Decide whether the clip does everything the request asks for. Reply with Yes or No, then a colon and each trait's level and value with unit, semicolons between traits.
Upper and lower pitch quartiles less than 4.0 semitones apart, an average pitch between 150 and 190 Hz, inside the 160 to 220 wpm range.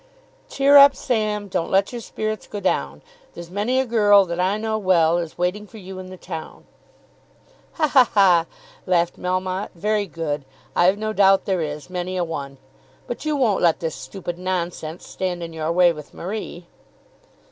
Yes: average, 3.4 semitones; medium, 185 Hz; average, 180 wpm